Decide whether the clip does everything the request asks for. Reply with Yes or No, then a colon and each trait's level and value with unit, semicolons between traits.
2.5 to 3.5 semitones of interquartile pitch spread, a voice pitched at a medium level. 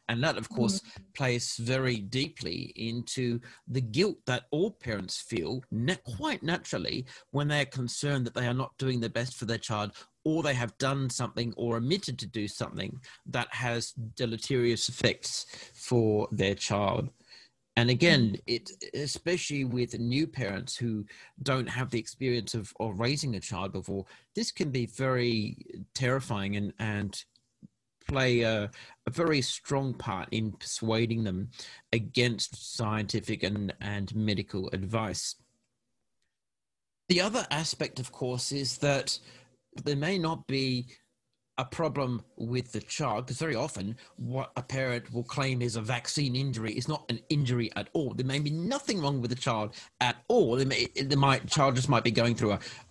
No: average, 3.2 semitones; low, 125 Hz